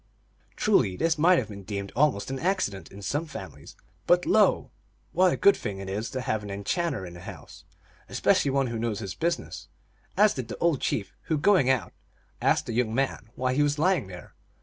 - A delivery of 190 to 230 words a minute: Yes, fast, 205 wpm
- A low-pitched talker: Yes, low, 125 Hz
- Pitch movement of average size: No, wide, 8.0 semitones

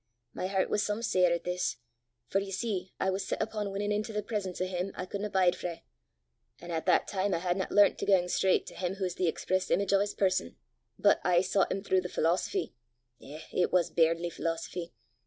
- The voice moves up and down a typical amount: No, narrow, 2.1 semitones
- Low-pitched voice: No, medium, 185 Hz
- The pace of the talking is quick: Yes, fast, 220 wpm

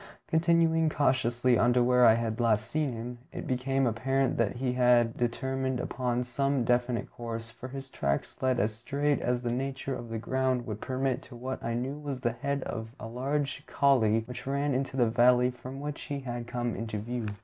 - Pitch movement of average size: No, narrow, 2.3 semitones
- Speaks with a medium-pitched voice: No, low, 125 Hz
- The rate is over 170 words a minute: Yes, average, 200 wpm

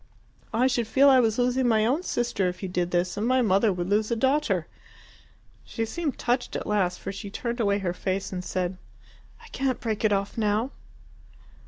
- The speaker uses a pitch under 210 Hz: No, high, 215 Hz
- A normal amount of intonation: Yes, average, 4.3 semitones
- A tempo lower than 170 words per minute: No, average, 200 wpm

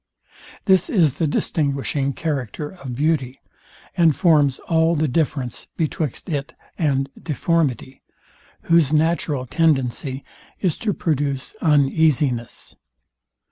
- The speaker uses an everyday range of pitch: Yes, average, 3.3 semitones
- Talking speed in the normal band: No, slow, 100 wpm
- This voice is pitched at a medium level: Yes, medium, 150 Hz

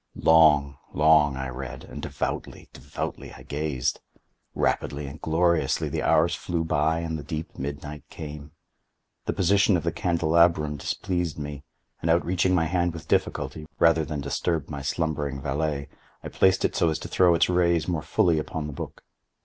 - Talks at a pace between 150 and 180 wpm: Yes, average, 165 wpm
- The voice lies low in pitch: Yes, very low, 80 Hz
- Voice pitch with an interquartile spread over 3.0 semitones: No, narrow, 2.6 semitones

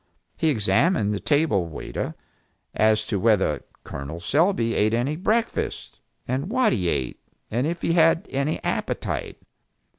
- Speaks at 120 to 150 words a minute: Yes, average, 140 wpm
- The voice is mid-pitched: No, low, 120 Hz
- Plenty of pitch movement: Yes, wide, 7.8 semitones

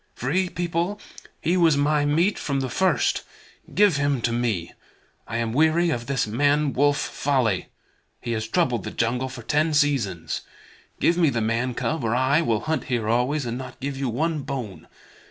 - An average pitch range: Yes, average, 4.8 semitones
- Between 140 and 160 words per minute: No, average, 180 wpm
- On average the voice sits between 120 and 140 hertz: Yes, low, 135 Hz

